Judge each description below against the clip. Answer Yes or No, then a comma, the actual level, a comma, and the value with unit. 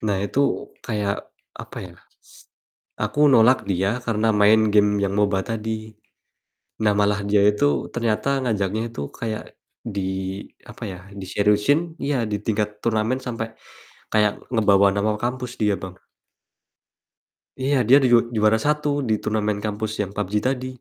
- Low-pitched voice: Yes, low, 105 Hz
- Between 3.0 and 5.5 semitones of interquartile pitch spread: No, narrow, 2.5 semitones